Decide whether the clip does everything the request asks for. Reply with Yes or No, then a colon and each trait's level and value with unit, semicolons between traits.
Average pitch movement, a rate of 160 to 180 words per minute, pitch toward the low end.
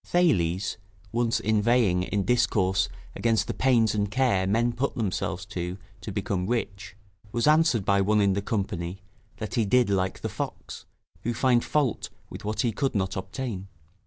Yes: average, 3.8 semitones; average, 165 wpm; low, 105 Hz